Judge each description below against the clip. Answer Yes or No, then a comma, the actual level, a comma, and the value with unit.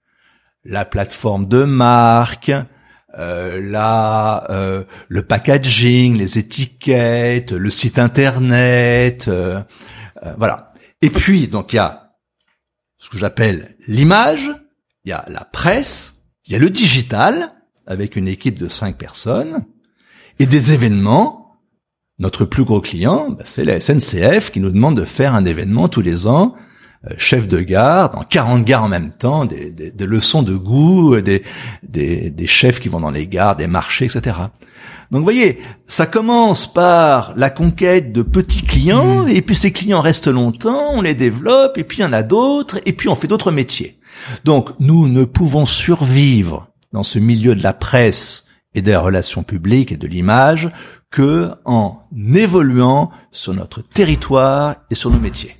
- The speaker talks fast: No, average, 165 wpm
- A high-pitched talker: No, low, 120 Hz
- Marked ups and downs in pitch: Yes, wide, 6.9 semitones